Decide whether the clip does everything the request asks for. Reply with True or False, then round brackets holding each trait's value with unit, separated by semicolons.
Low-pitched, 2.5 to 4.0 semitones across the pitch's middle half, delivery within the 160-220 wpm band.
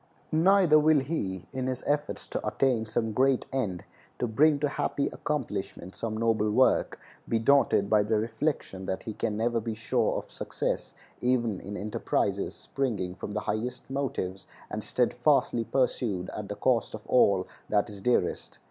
False (115 Hz; 4.4 semitones; 165 wpm)